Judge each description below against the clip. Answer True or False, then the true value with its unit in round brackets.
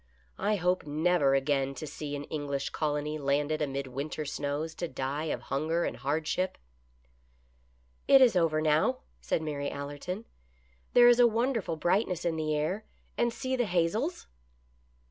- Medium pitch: True (155 Hz)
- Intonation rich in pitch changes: False (4.2 semitones)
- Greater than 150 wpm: True (160 wpm)